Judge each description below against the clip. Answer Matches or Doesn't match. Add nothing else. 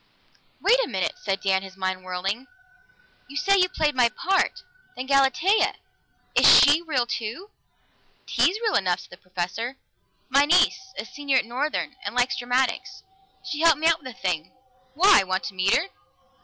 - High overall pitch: Matches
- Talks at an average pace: Matches